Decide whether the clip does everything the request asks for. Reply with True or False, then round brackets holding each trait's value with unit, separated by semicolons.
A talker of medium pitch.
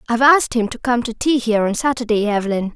False (235 Hz)